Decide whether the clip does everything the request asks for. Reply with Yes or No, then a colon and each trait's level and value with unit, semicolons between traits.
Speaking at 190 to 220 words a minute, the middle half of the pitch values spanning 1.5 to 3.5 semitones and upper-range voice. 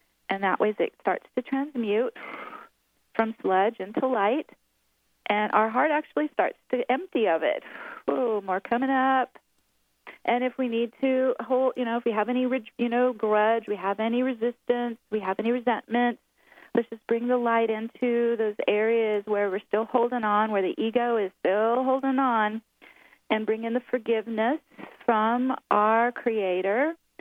No: average, 165 wpm; narrow, 2.5 semitones; high, 235 Hz